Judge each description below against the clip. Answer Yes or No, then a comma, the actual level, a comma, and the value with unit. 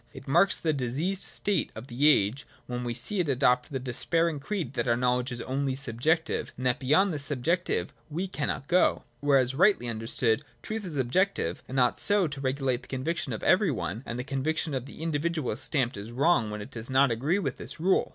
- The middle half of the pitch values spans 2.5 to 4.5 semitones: No, average, 4.9 semitones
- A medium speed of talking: No, fast, 210 wpm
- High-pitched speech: No, low, 135 Hz